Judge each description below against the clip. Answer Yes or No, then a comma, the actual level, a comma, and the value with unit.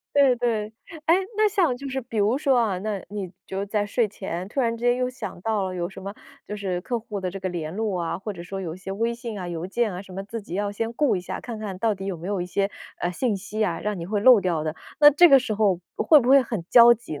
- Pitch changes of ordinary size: Yes, average, 4.2 semitones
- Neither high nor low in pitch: No, high, 210 Hz